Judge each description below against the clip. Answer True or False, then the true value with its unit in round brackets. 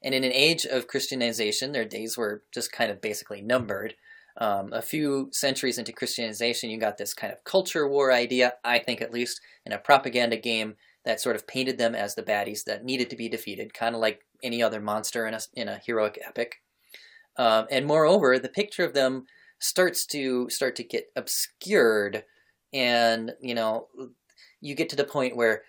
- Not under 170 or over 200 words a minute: True (195 wpm)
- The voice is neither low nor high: False (125 Hz)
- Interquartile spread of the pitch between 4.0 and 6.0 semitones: False (3.4 semitones)